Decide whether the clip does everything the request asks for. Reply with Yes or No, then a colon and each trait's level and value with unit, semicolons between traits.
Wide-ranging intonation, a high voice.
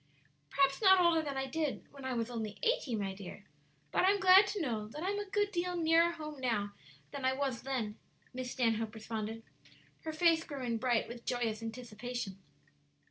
Yes: wide, 6.4 semitones; very high, 260 Hz